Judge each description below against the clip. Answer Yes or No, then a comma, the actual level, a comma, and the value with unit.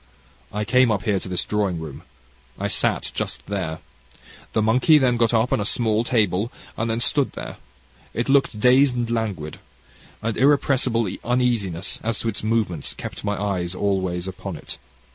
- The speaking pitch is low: Yes, low, 110 Hz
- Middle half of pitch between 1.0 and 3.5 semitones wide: No, average, 4.0 semitones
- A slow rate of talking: No, average, 165 wpm